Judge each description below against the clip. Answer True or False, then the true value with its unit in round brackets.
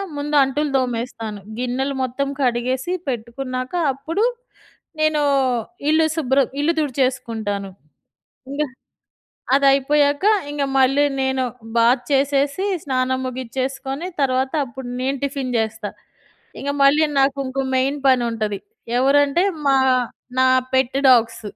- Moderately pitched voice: False (265 Hz)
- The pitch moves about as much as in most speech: False (1.9 semitones)